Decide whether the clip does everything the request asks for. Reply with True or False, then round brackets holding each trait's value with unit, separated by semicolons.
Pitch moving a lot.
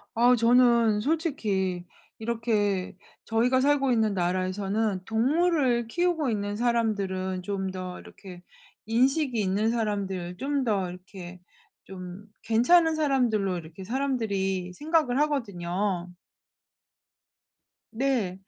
False (5.0 semitones)